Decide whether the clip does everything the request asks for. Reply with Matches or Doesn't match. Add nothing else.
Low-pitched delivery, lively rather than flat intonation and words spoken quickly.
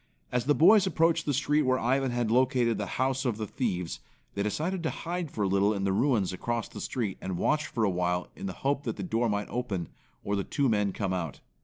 Matches